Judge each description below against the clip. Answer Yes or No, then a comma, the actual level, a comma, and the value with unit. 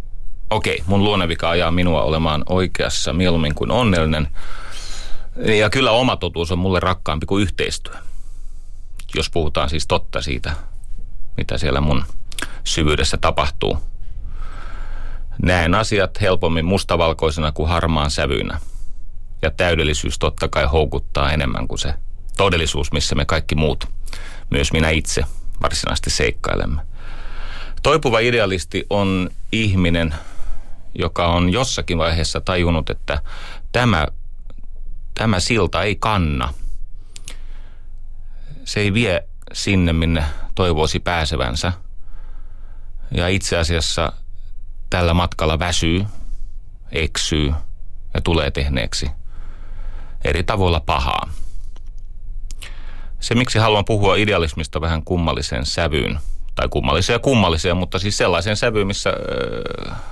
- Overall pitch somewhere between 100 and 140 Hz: No, very low, 90 Hz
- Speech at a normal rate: Yes, average, 105 wpm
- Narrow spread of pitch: No, average, 3.1 semitones